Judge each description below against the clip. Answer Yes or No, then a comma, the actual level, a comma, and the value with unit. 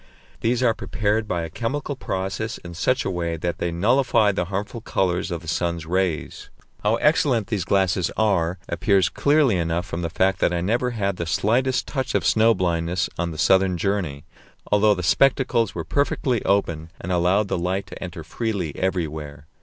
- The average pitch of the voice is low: Yes, very low, 95 Hz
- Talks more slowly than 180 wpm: No, average, 185 wpm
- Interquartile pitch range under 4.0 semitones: No, average, 4.5 semitones